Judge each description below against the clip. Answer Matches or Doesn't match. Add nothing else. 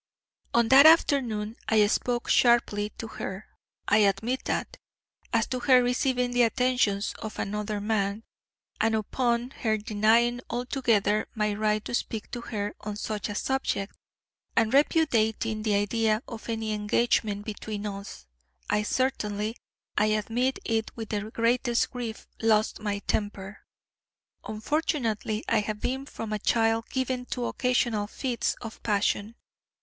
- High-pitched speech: Matches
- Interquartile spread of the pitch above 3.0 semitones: Doesn't match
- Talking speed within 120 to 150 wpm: Matches